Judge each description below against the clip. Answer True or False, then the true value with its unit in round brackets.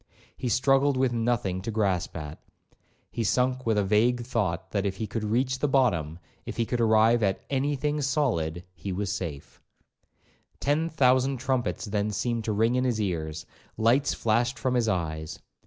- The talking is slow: False (175 wpm)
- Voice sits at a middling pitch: False (115 Hz)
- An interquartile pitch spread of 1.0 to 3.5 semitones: False (4.8 semitones)